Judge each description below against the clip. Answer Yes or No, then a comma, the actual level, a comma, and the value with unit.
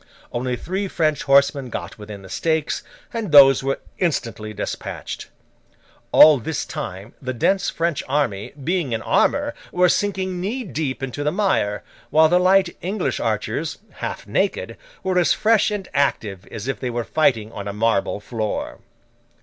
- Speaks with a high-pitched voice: No, medium, 145 Hz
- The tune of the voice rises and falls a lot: Yes, wide, 7.7 semitones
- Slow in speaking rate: No, average, 160 wpm